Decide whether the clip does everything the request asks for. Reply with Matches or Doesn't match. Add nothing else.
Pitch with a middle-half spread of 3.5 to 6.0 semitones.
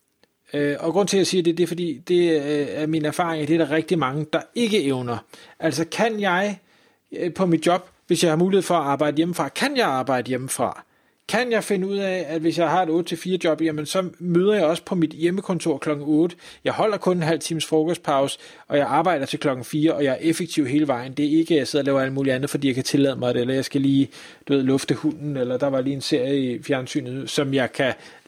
Matches